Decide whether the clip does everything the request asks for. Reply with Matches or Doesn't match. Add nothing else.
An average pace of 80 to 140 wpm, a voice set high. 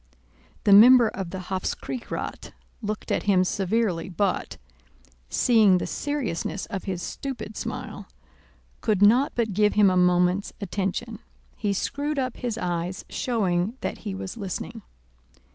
Matches